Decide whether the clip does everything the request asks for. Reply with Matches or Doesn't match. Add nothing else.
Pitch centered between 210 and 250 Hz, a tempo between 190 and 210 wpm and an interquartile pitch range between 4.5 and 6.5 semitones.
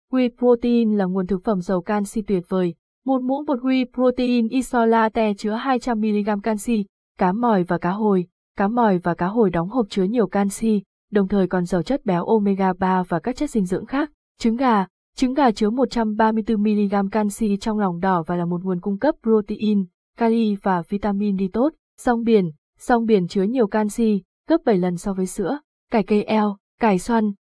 Doesn't match